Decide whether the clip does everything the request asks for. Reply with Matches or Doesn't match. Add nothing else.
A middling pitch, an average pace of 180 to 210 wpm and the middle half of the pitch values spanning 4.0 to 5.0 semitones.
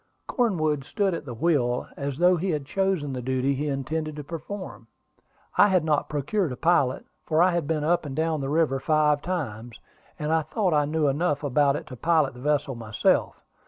Doesn't match